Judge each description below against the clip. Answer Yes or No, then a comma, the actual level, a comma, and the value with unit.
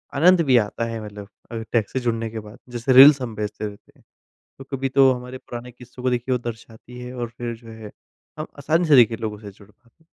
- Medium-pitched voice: No, low, 120 Hz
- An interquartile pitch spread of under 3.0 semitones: Yes, narrow, 2.6 semitones